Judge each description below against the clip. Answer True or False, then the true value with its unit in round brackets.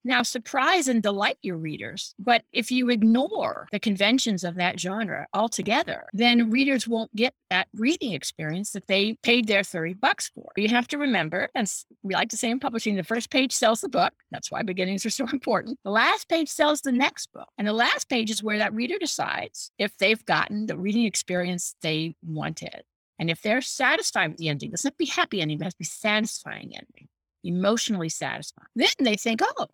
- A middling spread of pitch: True (4.9 semitones)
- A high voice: True (225 Hz)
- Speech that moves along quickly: True (210 wpm)